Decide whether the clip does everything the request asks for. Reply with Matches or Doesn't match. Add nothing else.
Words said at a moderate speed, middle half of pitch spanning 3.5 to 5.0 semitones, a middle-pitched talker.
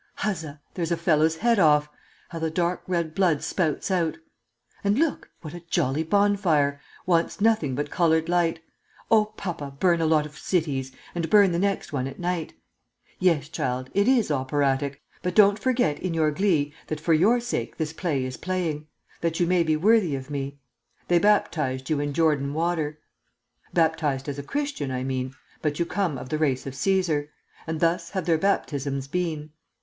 Matches